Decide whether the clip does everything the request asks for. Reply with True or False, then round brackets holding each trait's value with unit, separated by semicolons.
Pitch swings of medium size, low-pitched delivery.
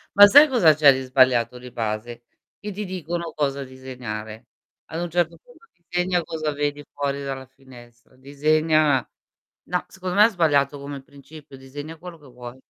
False (4.4 semitones; 145 Hz)